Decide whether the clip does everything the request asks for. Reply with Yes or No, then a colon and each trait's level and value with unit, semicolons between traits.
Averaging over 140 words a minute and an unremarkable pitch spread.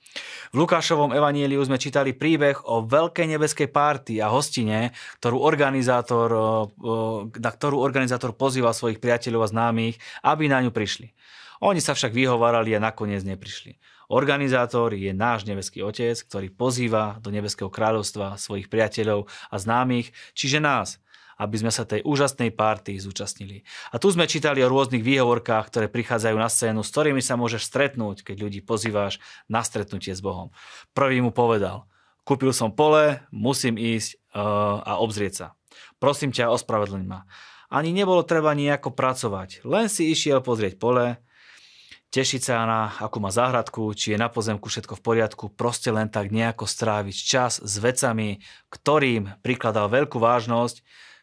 Yes: average, 150 wpm; average, 3.8 semitones